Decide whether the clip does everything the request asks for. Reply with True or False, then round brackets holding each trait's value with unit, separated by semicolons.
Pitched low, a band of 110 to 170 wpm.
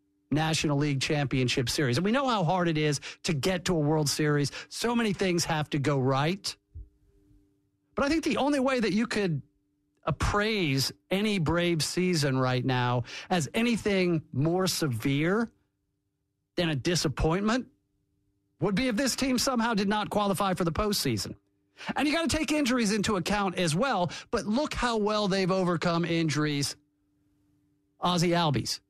False (165 Hz; 160 wpm)